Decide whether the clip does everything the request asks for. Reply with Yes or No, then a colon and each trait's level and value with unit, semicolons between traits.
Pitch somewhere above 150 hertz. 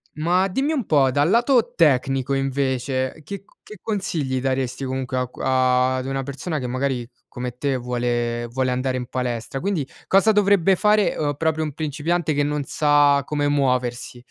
No: medium, 140 Hz